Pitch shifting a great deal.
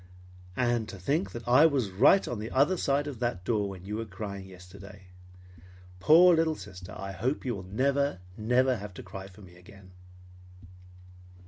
Yes: wide, 5.7 semitones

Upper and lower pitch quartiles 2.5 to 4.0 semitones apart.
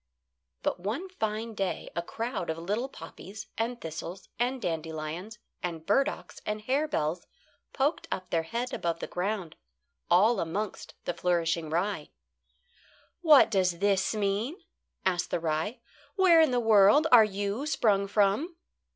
No: wide, 5.5 semitones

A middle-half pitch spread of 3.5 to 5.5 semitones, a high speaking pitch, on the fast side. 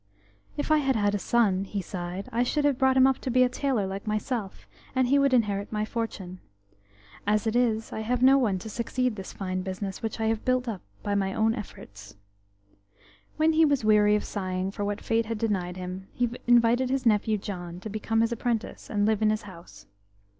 Yes: average, 3.9 semitones; high, 215 Hz; fast, 220 wpm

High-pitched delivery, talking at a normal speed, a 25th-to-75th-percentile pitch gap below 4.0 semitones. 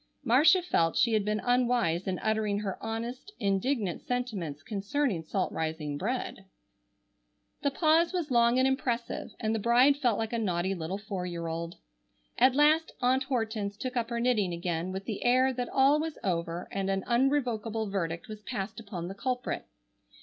No: high, 220 Hz; average, 170 wpm; average, 4.9 semitones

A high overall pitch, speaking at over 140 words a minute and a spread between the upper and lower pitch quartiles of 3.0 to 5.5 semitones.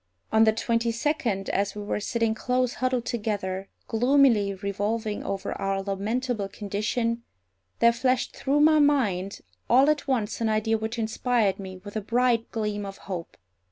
Yes: high, 220 Hz; average, 160 wpm; average, 3.5 semitones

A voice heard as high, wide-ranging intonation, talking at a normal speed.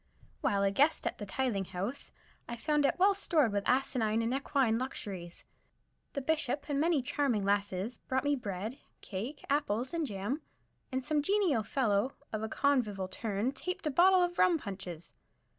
Yes: very high, 255 Hz; wide, 6.1 semitones; average, 170 wpm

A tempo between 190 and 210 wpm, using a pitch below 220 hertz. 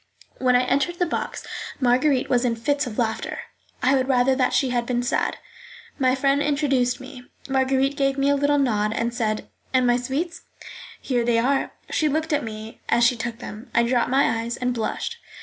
No: average, 200 wpm; very high, 255 Hz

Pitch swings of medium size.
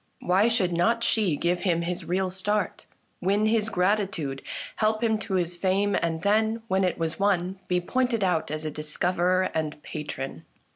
Yes: average, 3.6 semitones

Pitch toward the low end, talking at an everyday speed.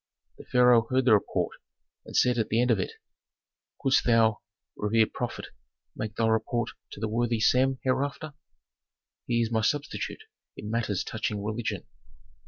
Yes: low, 115 Hz; average, 155 wpm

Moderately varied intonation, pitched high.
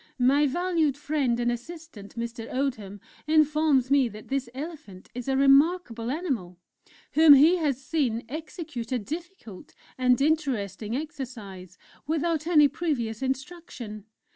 Yes: average, 4.9 semitones; very high, 270 Hz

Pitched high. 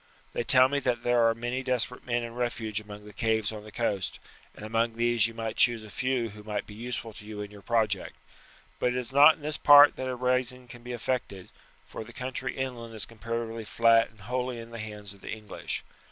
No: low, 115 Hz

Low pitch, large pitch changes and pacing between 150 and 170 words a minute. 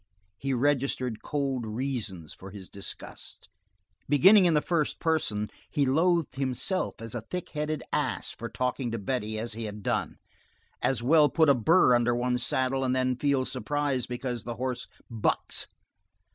No: low, 130 Hz; average, 3.9 semitones; average, 160 wpm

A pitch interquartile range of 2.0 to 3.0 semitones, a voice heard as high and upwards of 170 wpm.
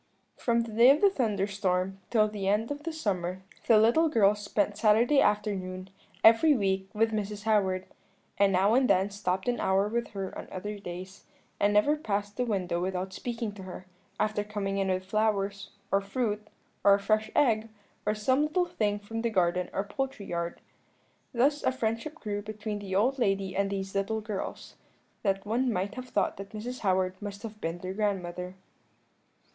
Yes: average, 2.7 semitones; high, 205 Hz; average, 185 wpm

